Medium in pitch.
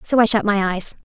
No: high, 210 Hz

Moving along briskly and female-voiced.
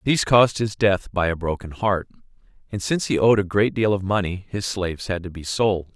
No: fast, 230 wpm; male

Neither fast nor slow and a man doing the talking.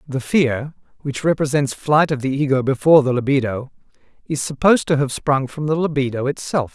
Yes: average, 180 wpm; male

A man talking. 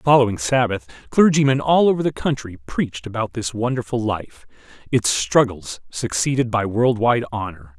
Yes: male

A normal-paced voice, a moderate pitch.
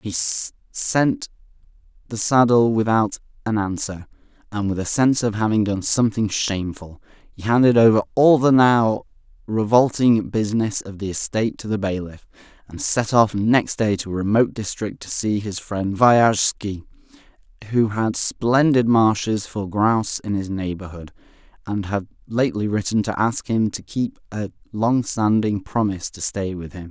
No: average, 155 wpm; low, 105 Hz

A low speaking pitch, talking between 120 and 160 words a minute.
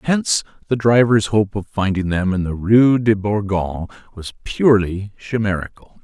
Yes: low, 105 Hz; average, 150 wpm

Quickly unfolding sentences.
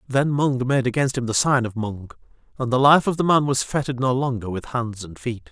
Yes: fast, 250 wpm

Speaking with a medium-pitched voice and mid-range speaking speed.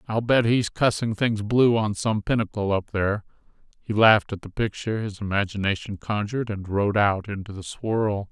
No: low, 105 Hz; average, 180 wpm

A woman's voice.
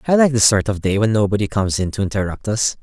No: male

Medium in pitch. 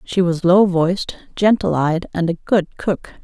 Yes: medium, 180 Hz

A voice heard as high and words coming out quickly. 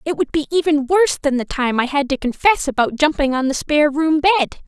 Yes: very high, 295 Hz; fast, 245 wpm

